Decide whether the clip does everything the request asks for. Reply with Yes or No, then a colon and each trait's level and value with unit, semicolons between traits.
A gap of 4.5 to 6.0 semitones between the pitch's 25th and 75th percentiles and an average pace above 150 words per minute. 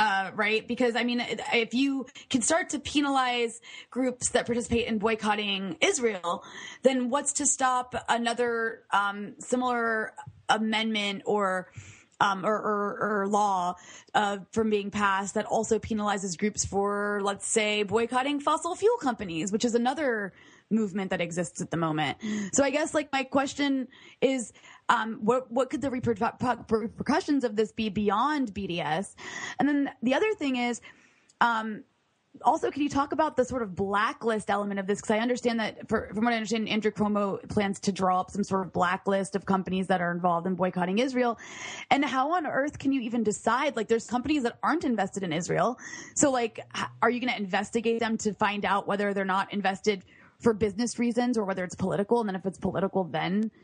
No: average, 3.8 semitones; average, 185 wpm